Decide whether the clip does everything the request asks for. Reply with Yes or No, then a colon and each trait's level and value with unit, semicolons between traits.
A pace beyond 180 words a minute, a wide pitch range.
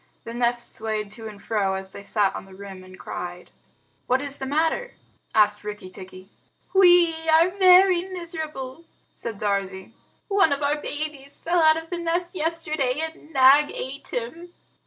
No: average, 165 wpm; wide, 7.9 semitones